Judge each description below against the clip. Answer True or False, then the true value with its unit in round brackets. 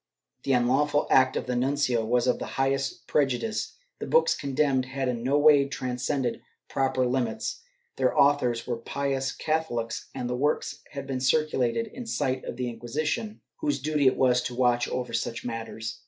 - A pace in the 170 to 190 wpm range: True (175 wpm)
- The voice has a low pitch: True (130 Hz)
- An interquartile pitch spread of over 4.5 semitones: False (2.7 semitones)